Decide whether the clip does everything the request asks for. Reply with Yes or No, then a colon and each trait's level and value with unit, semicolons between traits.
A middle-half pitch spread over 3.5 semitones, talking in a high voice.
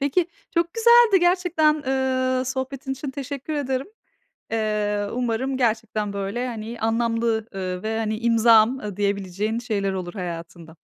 Yes: average, 4.3 semitones; high, 230 Hz